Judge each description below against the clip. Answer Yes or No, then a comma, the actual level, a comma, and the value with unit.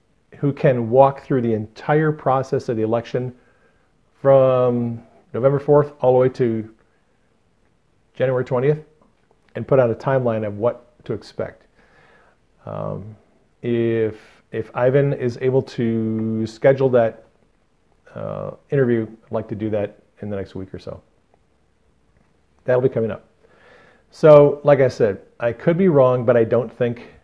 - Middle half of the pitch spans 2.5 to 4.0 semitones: Yes, average, 3.2 semitones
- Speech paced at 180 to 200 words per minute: No, average, 145 wpm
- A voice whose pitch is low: Yes, low, 120 Hz